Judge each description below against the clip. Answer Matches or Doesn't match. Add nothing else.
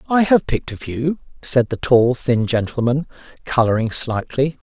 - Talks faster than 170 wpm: Doesn't match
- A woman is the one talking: Doesn't match